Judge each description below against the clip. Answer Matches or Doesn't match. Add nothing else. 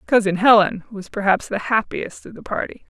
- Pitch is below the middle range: Doesn't match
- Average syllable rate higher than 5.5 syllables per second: Doesn't match